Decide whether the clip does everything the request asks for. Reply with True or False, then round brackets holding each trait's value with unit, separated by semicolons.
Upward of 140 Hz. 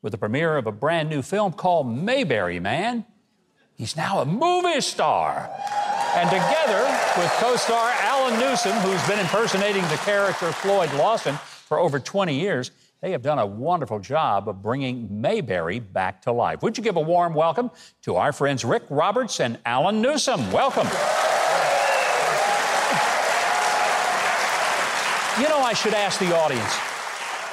True (190 Hz)